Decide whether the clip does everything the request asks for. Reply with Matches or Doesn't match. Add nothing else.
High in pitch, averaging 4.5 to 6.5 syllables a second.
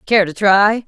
Doesn't match